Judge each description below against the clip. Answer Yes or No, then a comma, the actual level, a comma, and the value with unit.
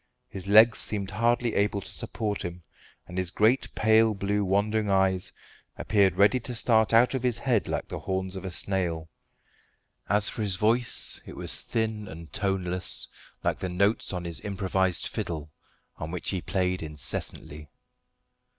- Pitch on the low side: Yes, low, 100 Hz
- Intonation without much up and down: No, average, 3.2 semitones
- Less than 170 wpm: Yes, average, 160 wpm